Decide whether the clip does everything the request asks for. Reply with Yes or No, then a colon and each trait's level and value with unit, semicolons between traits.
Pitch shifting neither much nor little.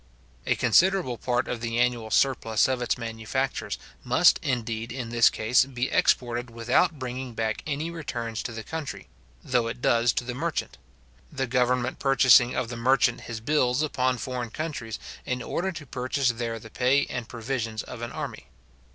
No: narrow, 2.3 semitones